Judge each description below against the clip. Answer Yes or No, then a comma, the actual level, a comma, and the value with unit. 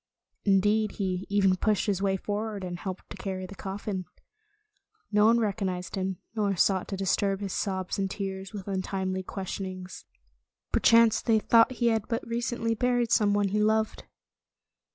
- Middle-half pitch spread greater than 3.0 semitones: No, narrow, 2.4 semitones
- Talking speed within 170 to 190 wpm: No, average, 160 wpm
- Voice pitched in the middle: No, high, 200 Hz